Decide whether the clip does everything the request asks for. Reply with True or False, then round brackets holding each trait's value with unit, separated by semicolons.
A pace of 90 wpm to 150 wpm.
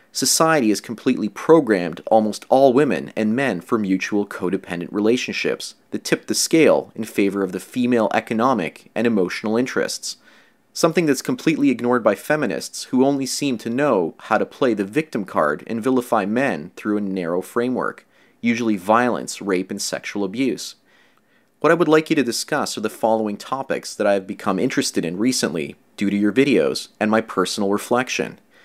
False (170 wpm)